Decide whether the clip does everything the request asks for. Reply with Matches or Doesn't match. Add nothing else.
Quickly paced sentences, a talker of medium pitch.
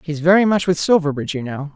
Matches